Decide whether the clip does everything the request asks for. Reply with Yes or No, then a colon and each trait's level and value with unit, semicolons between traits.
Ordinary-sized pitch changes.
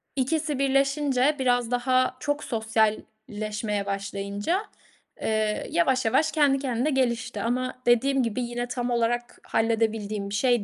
Yes: average, 3.4 semitones